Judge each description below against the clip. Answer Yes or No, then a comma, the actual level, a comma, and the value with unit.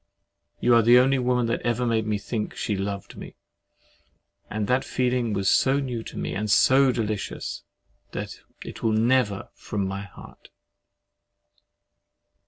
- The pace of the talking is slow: No, average, 150 wpm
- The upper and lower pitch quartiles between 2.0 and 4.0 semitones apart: Yes, average, 3.1 semitones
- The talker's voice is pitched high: No, low, 115 Hz